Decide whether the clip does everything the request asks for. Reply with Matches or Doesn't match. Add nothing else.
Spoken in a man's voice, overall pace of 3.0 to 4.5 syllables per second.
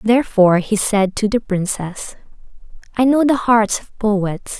Doesn't match